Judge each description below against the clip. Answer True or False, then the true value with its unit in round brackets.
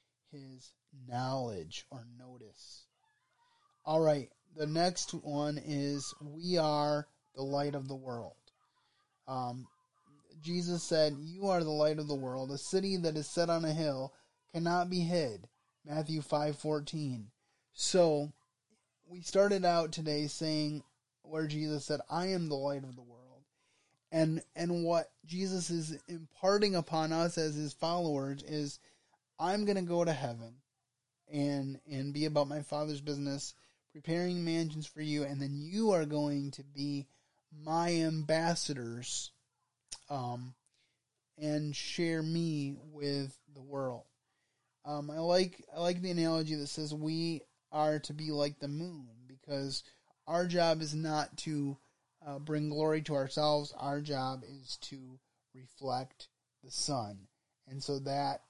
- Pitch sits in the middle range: True (150 Hz)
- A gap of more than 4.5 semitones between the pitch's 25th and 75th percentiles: False (2.9 semitones)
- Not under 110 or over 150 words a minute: True (145 wpm)